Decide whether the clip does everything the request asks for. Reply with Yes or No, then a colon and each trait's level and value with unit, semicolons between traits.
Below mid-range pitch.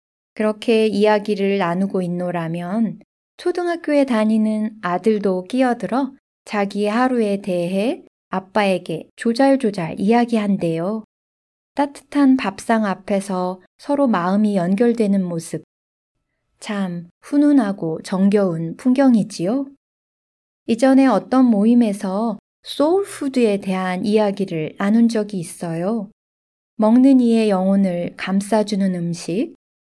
No: high, 210 Hz